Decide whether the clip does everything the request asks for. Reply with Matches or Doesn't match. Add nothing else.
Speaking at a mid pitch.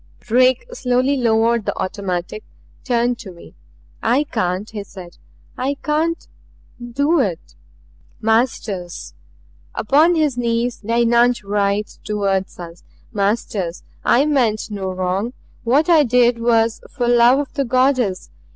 Doesn't match